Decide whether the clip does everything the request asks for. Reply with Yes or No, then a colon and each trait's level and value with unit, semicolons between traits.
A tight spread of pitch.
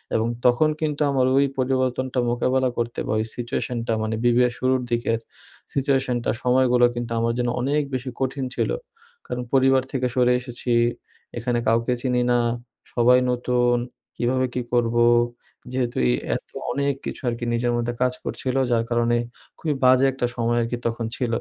Yes: narrow, 1.6 semitones